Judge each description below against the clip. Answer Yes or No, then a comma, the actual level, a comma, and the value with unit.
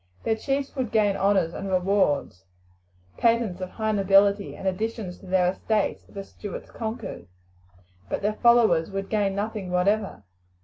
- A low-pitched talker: No, high, 200 Hz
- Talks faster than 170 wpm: No, average, 150 wpm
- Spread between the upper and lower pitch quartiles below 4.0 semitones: Yes, average, 2.8 semitones